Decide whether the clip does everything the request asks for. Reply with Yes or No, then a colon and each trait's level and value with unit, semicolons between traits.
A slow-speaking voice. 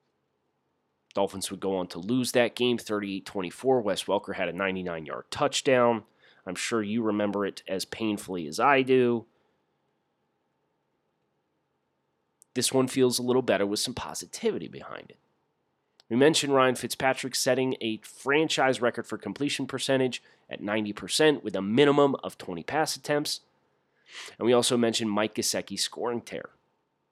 No: average, 145 wpm